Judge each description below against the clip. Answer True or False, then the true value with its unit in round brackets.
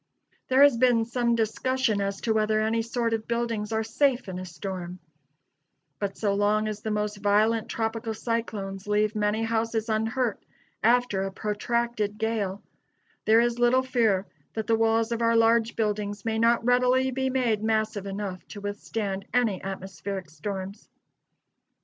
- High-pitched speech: True (220 Hz)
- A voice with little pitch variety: True (2.3 semitones)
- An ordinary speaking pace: True (155 wpm)